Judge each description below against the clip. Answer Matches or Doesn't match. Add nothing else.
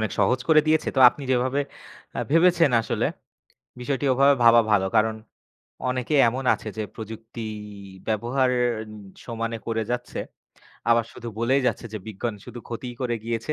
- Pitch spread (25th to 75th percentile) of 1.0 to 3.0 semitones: Matches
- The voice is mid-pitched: Doesn't match